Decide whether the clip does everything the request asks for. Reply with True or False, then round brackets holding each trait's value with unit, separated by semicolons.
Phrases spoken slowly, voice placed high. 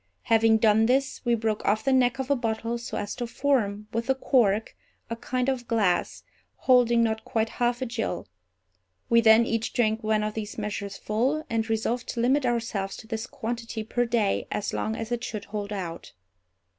False (195 wpm; 230 Hz)